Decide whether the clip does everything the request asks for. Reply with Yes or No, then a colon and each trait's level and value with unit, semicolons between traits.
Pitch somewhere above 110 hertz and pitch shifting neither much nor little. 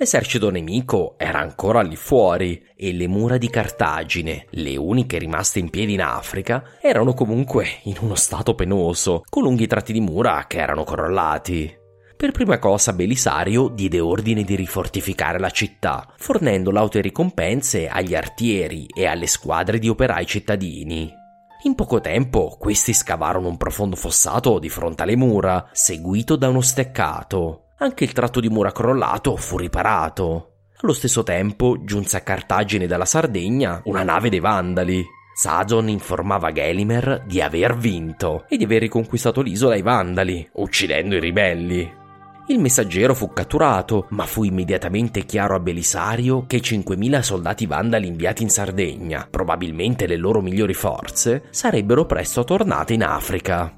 No: low, 100 Hz; average, 4.0 semitones